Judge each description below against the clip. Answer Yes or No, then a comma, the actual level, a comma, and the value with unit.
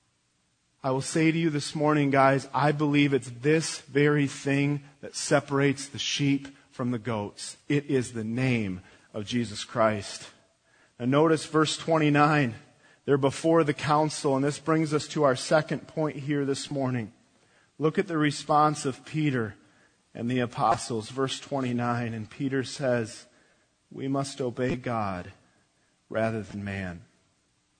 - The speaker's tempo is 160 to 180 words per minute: No, average, 145 wpm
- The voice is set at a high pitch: No, low, 135 Hz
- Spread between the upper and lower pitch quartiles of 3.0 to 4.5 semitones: Yes, average, 3.8 semitones